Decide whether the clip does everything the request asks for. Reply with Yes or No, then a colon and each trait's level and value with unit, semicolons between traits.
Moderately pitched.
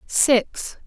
No: very high, 250 Hz